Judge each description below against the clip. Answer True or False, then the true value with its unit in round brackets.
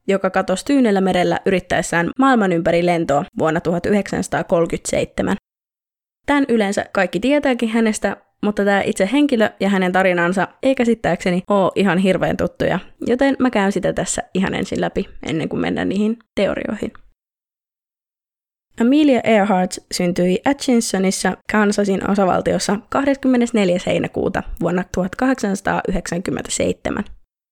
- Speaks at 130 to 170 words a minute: False (110 wpm)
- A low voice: False (200 Hz)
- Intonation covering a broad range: False (4.3 semitones)